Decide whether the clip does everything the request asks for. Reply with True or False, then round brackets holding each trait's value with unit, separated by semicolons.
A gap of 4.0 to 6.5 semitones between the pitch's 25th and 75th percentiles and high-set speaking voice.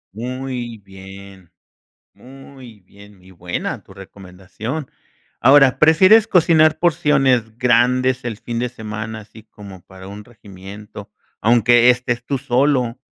False (4.4 semitones; 120 Hz)